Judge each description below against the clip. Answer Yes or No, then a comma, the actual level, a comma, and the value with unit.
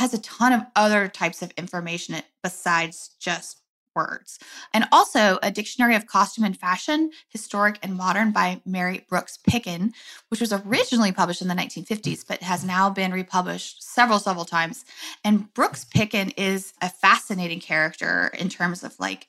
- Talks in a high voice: Yes, high, 195 Hz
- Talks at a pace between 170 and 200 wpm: No, average, 160 wpm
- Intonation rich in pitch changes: No, average, 3.7 semitones